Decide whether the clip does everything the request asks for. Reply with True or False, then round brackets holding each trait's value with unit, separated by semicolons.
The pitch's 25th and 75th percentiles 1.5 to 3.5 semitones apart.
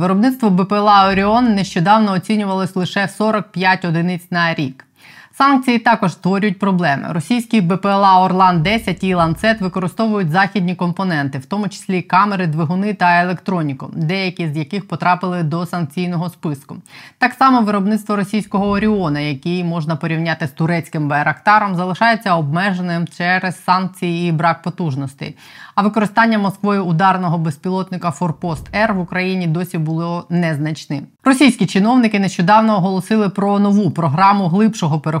True (3.1 semitones)